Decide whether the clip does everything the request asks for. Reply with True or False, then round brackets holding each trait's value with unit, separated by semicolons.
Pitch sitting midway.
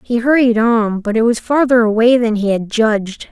False (230 Hz)